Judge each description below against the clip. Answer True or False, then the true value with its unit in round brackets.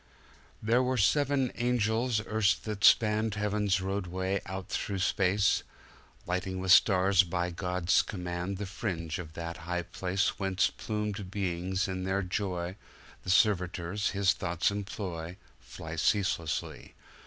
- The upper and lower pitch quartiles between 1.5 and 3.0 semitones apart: True (2.5 semitones)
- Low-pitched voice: True (95 Hz)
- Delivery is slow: True (120 wpm)